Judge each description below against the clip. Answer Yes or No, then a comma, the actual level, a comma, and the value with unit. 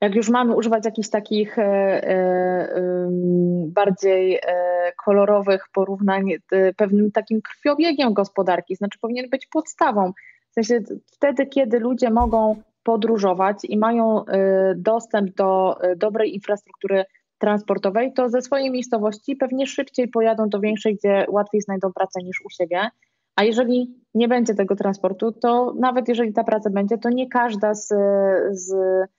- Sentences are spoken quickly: No, average, 145 wpm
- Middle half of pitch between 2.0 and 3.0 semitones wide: No, average, 3.5 semitones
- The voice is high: Yes, high, 210 Hz